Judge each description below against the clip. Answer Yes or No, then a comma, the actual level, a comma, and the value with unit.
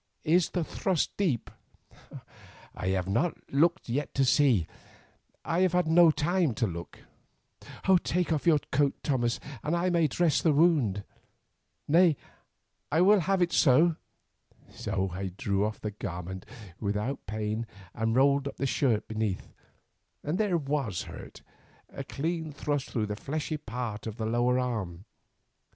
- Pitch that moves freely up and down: Yes, wide, 7.2 semitones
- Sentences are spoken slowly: No, average, 150 wpm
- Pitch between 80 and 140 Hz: Yes, low, 135 Hz